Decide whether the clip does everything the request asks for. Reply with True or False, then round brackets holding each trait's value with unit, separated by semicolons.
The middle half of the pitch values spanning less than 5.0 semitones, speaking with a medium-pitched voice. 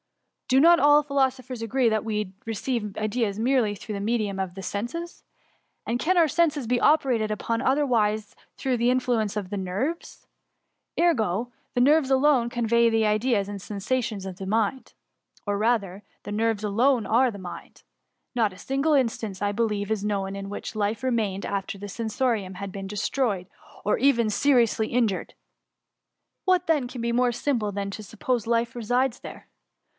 False (4.0 semitones; 225 Hz)